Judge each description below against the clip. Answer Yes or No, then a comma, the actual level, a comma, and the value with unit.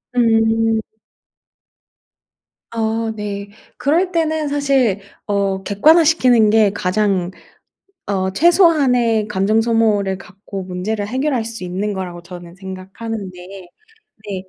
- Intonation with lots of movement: No, average, 3.8 semitones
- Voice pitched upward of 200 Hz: Yes, high, 215 Hz